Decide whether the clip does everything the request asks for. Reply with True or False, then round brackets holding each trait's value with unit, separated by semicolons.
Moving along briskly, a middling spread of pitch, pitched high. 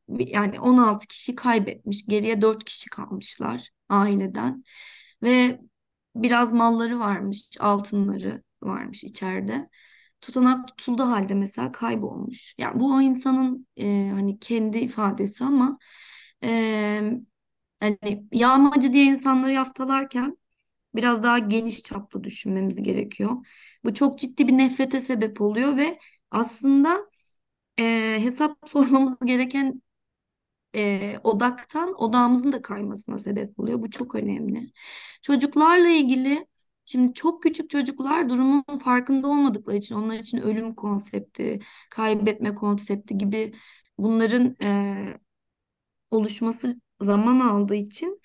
False (110 wpm; 3.9 semitones; 235 Hz)